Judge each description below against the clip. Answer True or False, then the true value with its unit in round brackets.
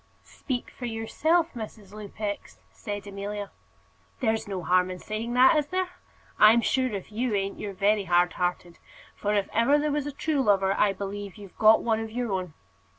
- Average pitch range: True (3.6 semitones)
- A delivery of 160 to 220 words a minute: True (185 wpm)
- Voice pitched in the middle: False (210 Hz)